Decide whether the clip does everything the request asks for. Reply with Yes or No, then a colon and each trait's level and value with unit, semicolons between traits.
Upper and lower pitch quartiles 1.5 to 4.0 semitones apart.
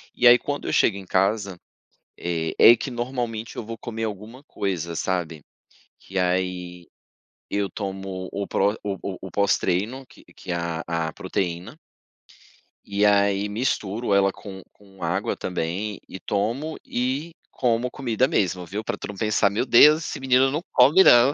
No: average, 4.4 semitones